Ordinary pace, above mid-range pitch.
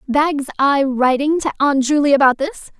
Yes: average, 170 wpm; very high, 285 Hz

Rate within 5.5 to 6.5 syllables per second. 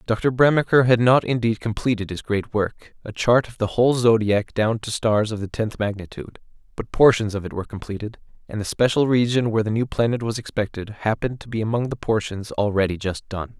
Yes: 5.8 syllables/s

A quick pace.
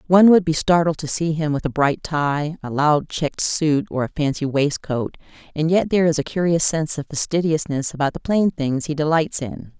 Yes: fast, 215 wpm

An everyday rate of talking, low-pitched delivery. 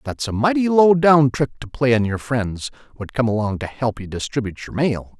No: fast, 230 wpm; low, 125 Hz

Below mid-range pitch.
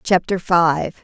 No: medium, 175 Hz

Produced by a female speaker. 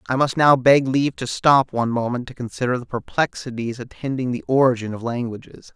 No: male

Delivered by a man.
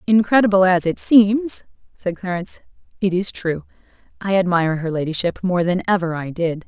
No: female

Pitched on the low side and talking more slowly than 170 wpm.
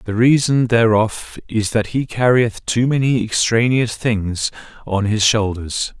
Yes: low, 115 Hz; average, 140 wpm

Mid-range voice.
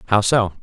No: low, 105 Hz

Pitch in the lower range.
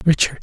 No: medium, 150 Hz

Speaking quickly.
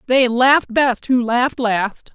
No: average, 170 wpm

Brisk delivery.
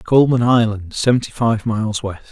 No: average, 155 wpm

